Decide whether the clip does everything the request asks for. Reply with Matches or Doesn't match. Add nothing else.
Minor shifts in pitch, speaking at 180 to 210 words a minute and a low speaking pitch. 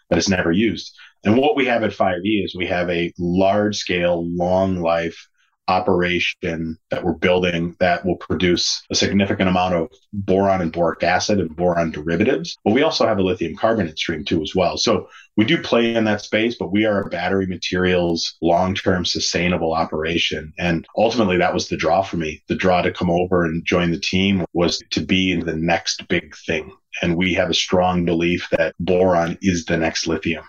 Matches